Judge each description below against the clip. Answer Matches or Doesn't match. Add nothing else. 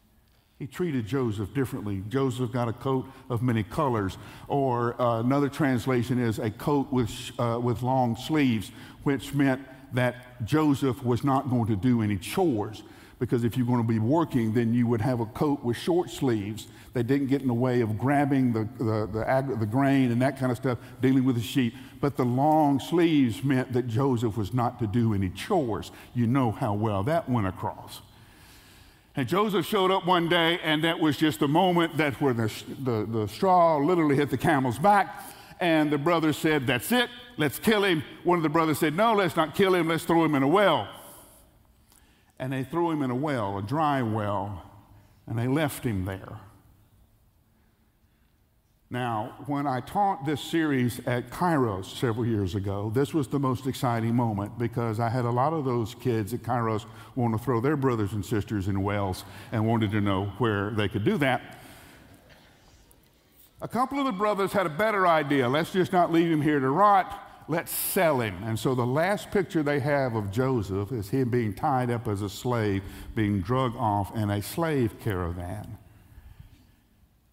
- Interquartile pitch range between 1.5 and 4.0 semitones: Doesn't match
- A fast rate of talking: Doesn't match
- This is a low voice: Matches